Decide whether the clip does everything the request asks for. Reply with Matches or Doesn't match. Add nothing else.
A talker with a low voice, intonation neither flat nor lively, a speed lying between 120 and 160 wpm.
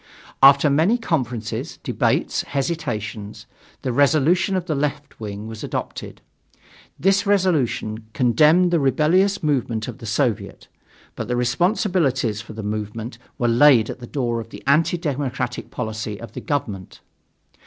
Doesn't match